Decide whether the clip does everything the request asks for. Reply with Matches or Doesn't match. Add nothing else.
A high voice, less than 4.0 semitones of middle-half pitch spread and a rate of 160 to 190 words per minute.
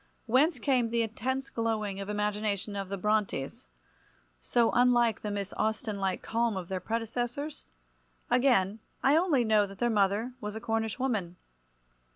Doesn't match